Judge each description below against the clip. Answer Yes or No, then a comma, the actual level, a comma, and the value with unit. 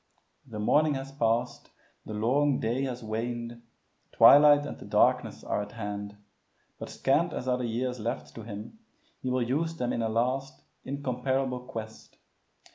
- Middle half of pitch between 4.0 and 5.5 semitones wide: No, average, 3.1 semitones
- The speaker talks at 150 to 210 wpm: Yes, average, 160 wpm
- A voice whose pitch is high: No, low, 125 Hz